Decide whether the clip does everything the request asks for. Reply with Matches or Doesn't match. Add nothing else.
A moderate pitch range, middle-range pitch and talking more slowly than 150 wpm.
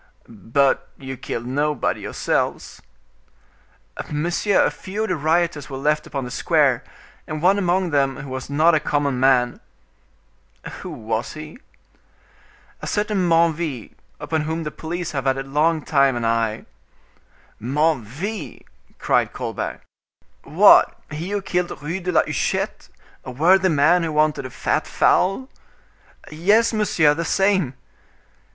Matches